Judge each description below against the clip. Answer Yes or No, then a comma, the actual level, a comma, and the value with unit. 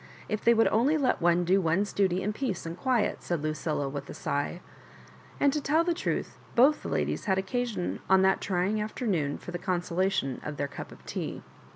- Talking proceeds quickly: Yes, fast, 210 wpm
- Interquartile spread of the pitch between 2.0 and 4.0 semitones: No, wide, 5.4 semitones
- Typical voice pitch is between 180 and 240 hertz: Yes, high, 190 Hz